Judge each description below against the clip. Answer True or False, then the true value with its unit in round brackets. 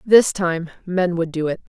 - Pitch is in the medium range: True (175 Hz)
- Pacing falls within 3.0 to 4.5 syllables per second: True (4.3 syllables/s)